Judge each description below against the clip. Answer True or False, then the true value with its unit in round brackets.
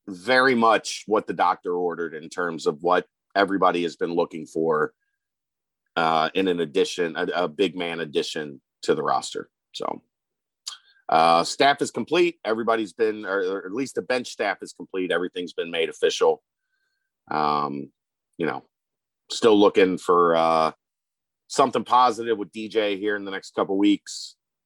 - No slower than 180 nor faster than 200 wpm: False (160 wpm)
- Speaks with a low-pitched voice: True (125 Hz)